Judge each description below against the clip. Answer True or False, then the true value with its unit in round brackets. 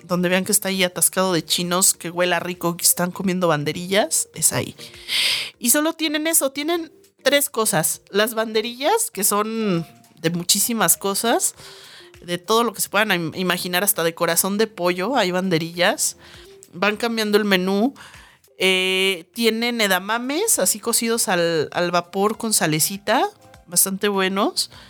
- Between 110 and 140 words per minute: False (150 wpm)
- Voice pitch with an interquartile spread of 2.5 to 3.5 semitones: False (4.3 semitones)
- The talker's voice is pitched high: True (195 Hz)